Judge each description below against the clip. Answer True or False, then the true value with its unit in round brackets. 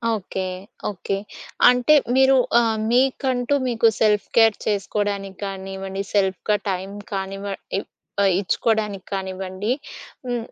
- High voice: True (205 Hz)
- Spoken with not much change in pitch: False (3.2 semitones)